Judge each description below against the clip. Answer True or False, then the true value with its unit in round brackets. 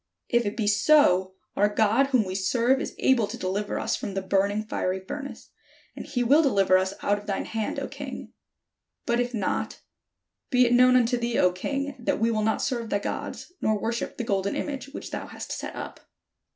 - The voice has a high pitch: True (220 Hz)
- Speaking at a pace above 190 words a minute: True (205 wpm)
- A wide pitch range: False (3.8 semitones)